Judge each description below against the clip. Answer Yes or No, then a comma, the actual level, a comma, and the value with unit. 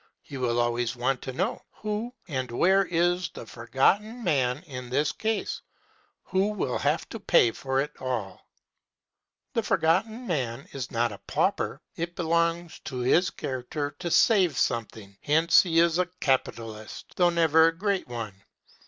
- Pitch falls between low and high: Yes, medium, 145 Hz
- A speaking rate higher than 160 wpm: No, average, 155 wpm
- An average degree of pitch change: No, wide, 6.3 semitones